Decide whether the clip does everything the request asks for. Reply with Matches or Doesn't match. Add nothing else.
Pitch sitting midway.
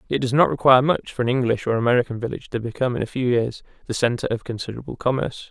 Doesn't match